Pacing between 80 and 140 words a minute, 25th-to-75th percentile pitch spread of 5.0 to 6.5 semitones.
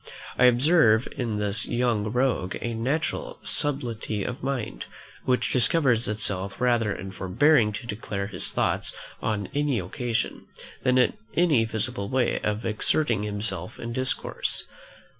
No: slow, 135 wpm; average, 3.6 semitones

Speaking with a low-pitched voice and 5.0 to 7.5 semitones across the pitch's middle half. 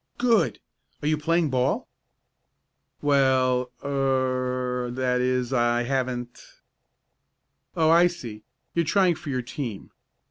No: low, 130 Hz; average, 3.2 semitones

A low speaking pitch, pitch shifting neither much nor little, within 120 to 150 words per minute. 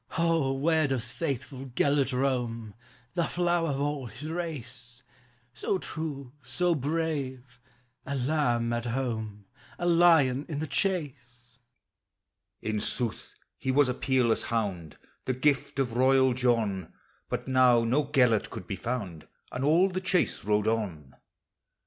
Yes: low, 130 Hz; average, 4.0 semitones; average, 145 wpm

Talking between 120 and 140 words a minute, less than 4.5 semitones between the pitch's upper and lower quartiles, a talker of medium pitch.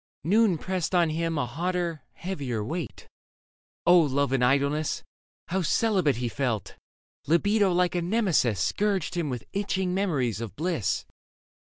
No: slow, 135 wpm; average, 5.2 semitones; medium, 165 Hz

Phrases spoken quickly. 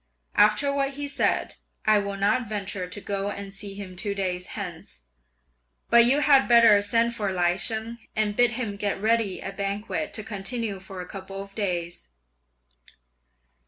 No: average, 165 wpm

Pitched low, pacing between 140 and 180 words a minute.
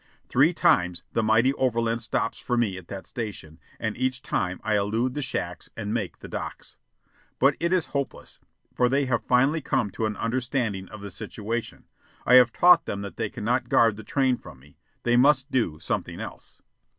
No: low, 115 Hz; average, 190 wpm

